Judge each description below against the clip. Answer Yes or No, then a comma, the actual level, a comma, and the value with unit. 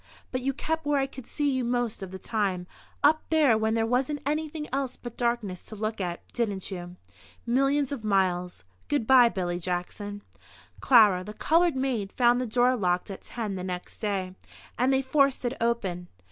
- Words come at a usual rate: Yes, average, 190 wpm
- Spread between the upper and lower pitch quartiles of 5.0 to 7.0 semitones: Yes, wide, 5.6 semitones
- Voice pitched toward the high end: Yes, high, 235 Hz